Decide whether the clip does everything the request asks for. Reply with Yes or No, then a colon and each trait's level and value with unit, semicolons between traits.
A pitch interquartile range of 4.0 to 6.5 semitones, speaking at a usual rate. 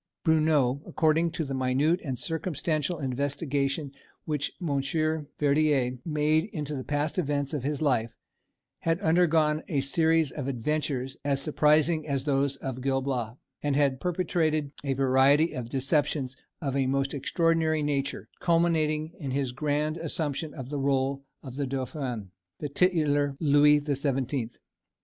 No: narrow, 2.5 semitones; average, 145 wpm